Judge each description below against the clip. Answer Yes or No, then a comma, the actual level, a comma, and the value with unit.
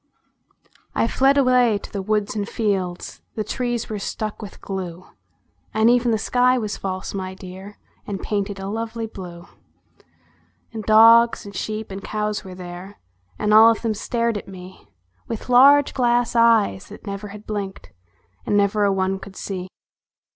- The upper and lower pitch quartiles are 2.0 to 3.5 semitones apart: Yes, average, 3.0 semitones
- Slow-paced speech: No, average, 165 wpm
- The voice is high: Yes, high, 210 Hz